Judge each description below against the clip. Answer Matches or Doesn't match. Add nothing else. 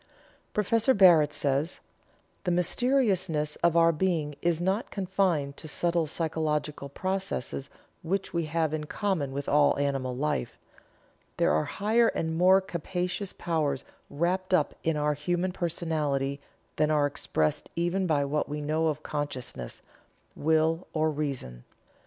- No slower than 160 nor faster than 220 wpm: Doesn't match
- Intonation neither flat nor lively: Matches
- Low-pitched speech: Doesn't match